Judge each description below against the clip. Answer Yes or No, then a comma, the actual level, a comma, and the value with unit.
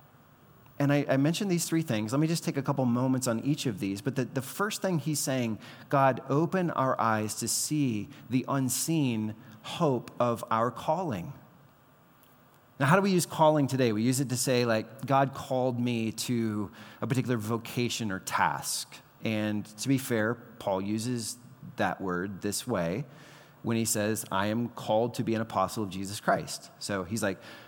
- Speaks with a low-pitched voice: Yes, low, 125 Hz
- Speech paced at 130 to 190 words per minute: Yes, average, 185 wpm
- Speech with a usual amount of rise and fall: Yes, average, 4.1 semitones